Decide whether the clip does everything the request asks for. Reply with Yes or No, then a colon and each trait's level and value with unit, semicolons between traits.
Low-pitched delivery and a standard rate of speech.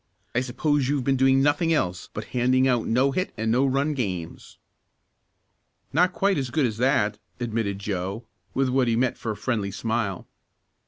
Yes: low, 125 Hz; average, 175 wpm